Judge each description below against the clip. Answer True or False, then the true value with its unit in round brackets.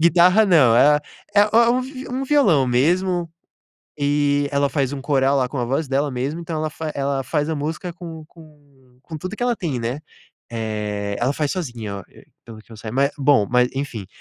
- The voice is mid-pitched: True (145 Hz)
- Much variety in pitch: False (4.9 semitones)